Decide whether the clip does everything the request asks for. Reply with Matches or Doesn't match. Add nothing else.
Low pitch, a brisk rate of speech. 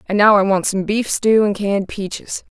Doesn't match